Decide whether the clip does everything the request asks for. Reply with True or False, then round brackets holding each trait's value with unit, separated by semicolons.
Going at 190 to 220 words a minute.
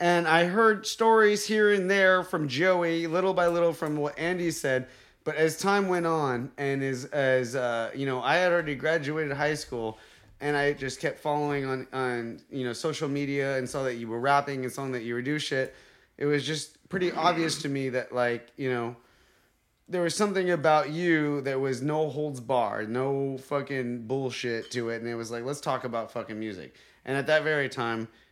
True (205 wpm)